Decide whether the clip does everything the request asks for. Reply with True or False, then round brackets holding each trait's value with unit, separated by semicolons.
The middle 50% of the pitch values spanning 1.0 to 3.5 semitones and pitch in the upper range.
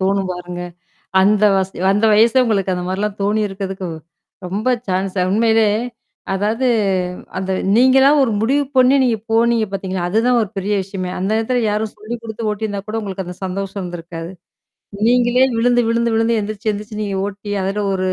True (2.9 semitones; 210 Hz)